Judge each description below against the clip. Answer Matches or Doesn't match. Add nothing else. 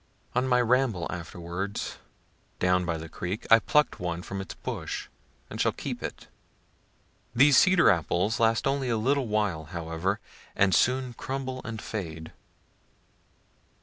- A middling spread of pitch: Doesn't match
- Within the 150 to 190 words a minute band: Doesn't match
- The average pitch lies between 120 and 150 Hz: Doesn't match